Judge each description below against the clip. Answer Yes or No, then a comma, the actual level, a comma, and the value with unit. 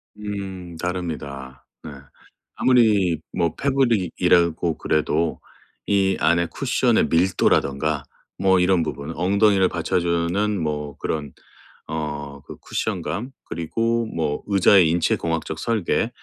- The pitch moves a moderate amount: Yes, average, 4.0 semitones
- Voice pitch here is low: Yes, very low, 85 Hz